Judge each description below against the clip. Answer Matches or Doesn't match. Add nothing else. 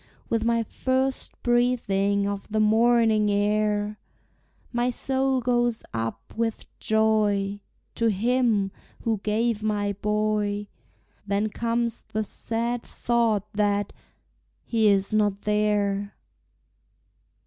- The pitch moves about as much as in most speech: Doesn't match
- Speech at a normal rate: Doesn't match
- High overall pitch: Matches